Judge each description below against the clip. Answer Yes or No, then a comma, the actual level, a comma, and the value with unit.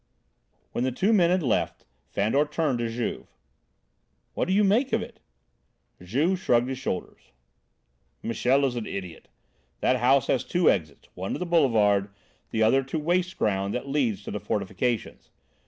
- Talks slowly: No, average, 165 wpm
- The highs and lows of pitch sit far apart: Yes, wide, 6.7 semitones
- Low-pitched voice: Yes, low, 125 Hz